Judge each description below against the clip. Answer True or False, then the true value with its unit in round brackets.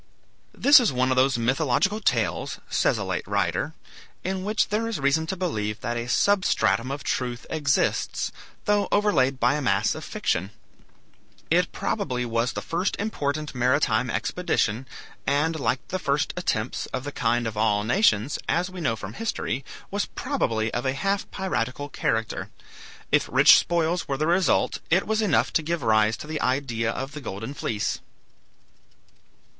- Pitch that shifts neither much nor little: False (7.2 semitones)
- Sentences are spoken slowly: False (165 wpm)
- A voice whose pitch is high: False (140 Hz)